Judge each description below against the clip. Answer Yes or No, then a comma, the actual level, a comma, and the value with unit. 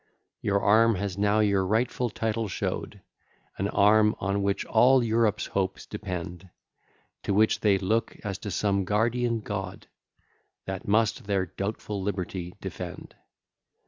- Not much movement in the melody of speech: Yes, narrow, 2.2 semitones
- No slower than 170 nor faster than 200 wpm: No, slow, 135 wpm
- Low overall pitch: Yes, low, 100 Hz